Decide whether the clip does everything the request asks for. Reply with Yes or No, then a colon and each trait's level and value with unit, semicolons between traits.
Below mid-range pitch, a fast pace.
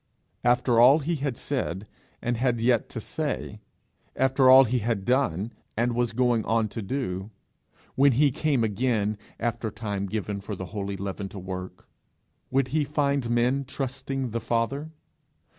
No: low, 120 Hz; average, 160 wpm